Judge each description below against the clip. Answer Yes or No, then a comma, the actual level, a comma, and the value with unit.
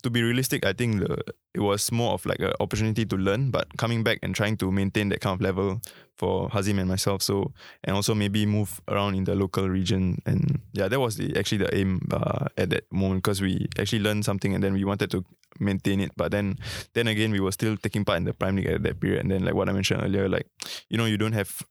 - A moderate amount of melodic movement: No, narrow, 2.2 semitones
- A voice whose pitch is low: Yes, low, 100 Hz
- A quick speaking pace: Yes, fast, 255 wpm